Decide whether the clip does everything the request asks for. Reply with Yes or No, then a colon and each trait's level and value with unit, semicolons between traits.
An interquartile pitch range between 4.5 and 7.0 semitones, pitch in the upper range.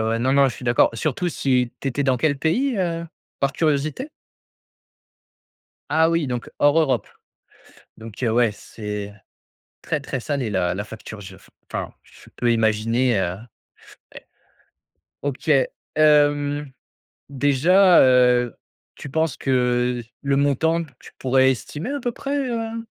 No: average, 4.9 semitones; low, 135 Hz